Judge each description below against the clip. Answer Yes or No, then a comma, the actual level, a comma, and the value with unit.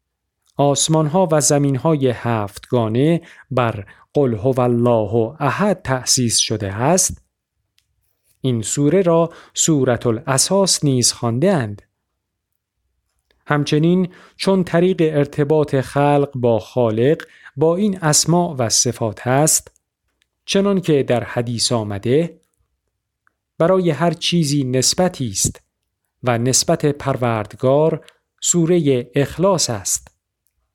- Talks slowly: Yes, slow, 95 wpm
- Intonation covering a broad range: Yes, wide, 5.7 semitones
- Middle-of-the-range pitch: No, low, 130 Hz